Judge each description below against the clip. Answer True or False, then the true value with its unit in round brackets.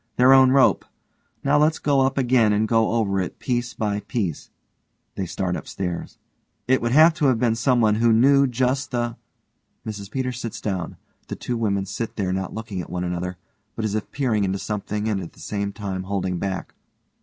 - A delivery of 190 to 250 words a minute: True (195 wpm)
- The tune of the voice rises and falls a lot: False (4.4 semitones)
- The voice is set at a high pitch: False (110 Hz)